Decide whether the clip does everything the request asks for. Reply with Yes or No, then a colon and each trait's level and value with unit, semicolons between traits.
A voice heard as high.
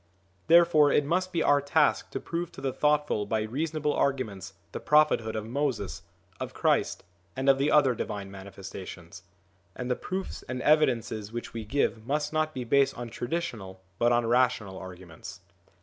No: low, 130 Hz